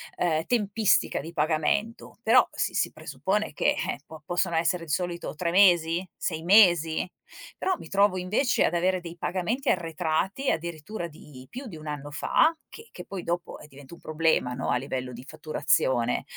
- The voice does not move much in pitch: No, average, 3.8 semitones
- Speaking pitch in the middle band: Yes, medium, 170 Hz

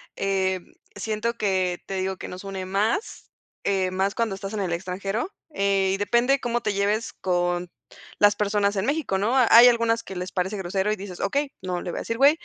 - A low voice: No, high, 200 Hz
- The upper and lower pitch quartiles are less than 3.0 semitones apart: No, average, 3.3 semitones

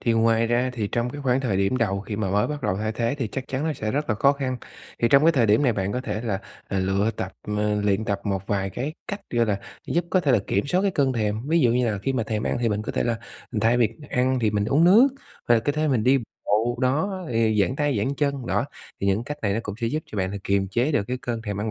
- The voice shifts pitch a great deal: No, average, 4.5 semitones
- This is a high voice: No, low, 115 Hz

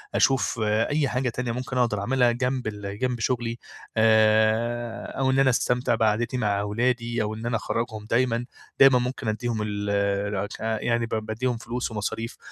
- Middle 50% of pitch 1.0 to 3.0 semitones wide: Yes, narrow, 2.5 semitones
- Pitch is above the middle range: No, low, 115 Hz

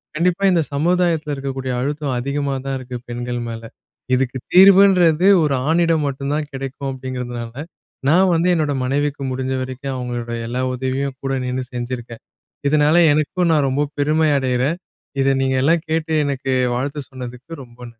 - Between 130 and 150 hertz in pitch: Yes, medium, 140 Hz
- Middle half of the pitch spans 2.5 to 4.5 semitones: Yes, average, 3.3 semitones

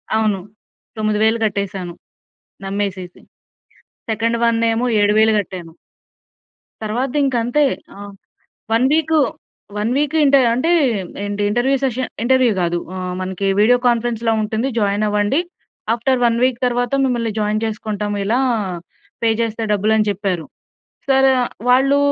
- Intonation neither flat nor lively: Yes, average, 3.2 semitones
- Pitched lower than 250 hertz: Yes, high, 225 Hz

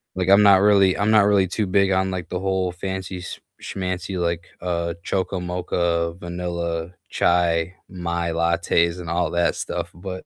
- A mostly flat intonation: Yes, narrow, 1.8 semitones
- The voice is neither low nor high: No, very low, 90 Hz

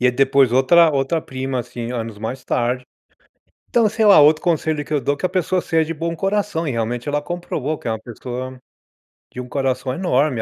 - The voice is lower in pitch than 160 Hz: Yes, medium, 140 Hz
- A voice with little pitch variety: No, average, 4.6 semitones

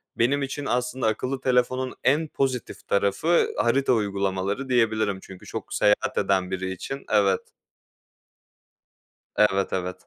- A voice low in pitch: Yes, low, 115 Hz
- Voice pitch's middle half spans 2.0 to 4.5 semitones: No, average, 4.9 semitones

